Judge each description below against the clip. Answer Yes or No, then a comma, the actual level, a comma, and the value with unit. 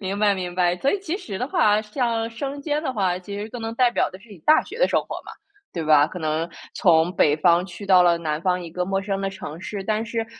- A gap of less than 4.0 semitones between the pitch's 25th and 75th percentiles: No, average, 4.4 semitones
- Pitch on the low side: No, high, 195 Hz